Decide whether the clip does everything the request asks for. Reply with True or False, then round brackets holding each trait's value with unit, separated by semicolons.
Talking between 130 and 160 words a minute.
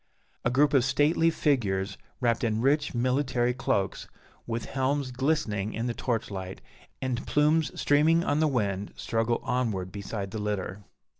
True (150 wpm)